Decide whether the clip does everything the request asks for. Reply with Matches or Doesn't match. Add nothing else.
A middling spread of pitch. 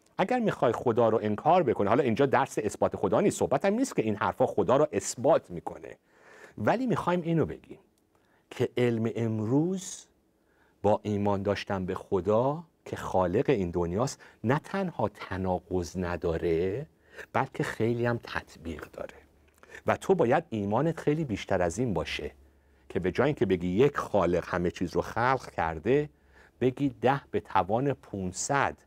Doesn't match